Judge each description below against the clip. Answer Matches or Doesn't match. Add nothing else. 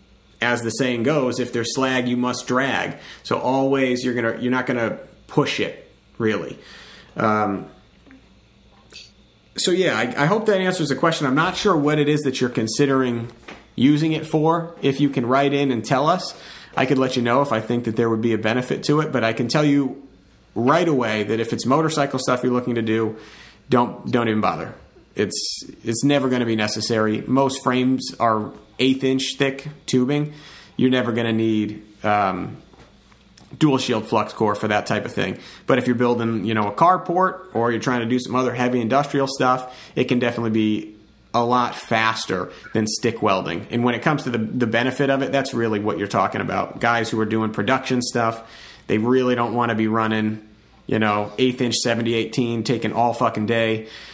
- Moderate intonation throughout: Matches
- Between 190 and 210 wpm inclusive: Matches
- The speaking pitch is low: Matches